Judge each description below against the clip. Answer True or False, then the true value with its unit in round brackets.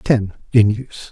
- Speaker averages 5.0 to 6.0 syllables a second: False (6.2 syllables/s)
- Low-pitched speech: True (110 Hz)